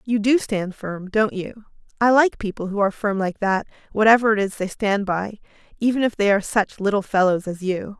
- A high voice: Yes, high, 205 Hz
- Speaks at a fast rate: Yes, fast, 220 wpm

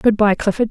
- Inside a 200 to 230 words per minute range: No, fast, 255 wpm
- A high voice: Yes, high, 210 Hz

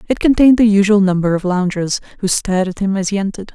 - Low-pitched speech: No, high, 200 Hz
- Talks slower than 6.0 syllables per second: No, 7.0 syllables/s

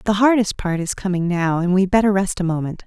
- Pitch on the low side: No, high, 190 Hz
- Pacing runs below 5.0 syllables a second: No, 5.9 syllables/s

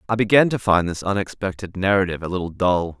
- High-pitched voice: No, very low, 95 Hz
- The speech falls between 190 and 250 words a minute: Yes, average, 200 wpm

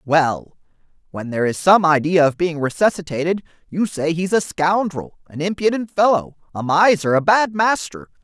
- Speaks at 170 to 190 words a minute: No, average, 160 wpm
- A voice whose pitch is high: No, medium, 170 Hz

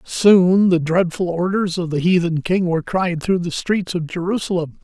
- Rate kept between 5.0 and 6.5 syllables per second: No, 4.7 syllables/s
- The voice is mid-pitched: Yes, medium, 175 Hz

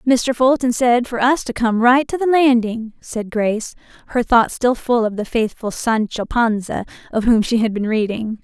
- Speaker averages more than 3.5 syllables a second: Yes, 4.6 syllables/s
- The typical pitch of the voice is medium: No, high, 235 Hz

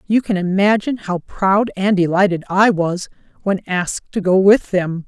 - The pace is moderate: Yes, average, 175 wpm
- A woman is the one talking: Yes, female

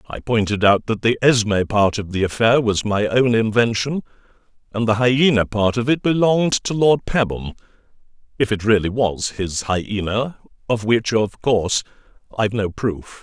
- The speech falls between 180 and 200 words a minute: No, average, 170 wpm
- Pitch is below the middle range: Yes, low, 110 Hz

